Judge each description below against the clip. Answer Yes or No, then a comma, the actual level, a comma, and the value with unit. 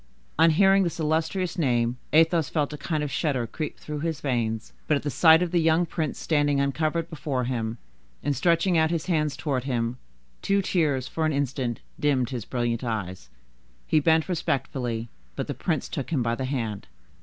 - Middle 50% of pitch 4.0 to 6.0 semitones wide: Yes, average, 4.5 semitones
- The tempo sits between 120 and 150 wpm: No, average, 190 wpm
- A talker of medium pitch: Yes, medium, 145 Hz